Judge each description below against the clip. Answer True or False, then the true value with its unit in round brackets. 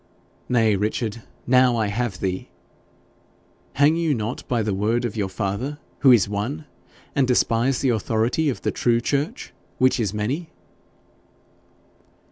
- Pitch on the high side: False (120 Hz)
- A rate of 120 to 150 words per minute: True (140 wpm)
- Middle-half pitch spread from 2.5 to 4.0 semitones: True (3.6 semitones)